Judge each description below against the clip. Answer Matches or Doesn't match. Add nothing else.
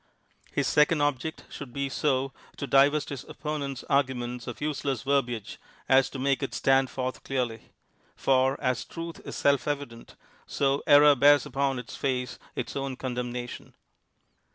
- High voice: Doesn't match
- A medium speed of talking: Matches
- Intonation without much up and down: Matches